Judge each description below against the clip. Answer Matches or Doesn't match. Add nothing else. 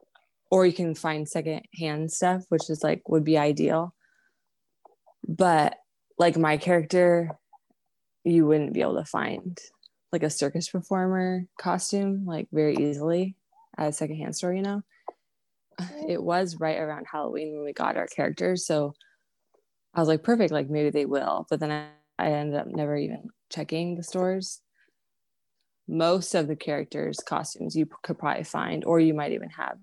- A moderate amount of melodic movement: Matches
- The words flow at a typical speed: Matches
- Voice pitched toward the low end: Doesn't match